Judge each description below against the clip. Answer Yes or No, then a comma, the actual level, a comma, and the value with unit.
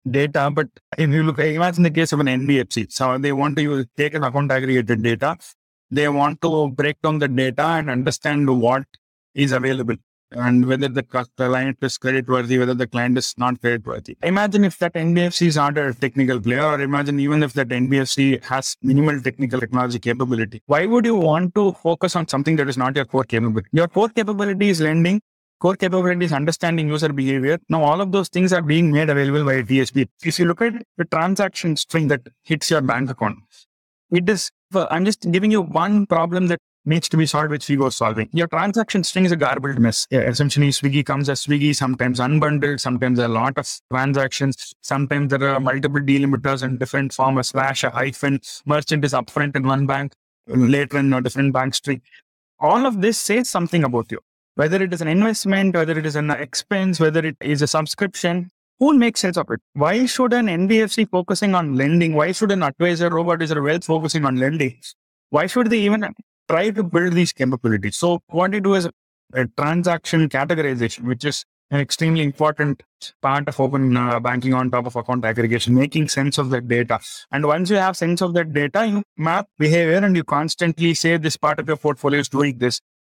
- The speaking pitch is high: No, medium, 145 Hz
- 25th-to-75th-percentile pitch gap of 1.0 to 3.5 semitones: No, average, 4.5 semitones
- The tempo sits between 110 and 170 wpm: No, fast, 205 wpm